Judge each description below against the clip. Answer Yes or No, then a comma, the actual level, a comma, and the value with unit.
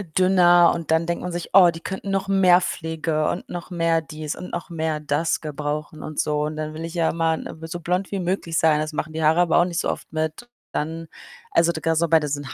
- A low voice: No, medium, 165 Hz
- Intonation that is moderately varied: No, narrow, 2.1 semitones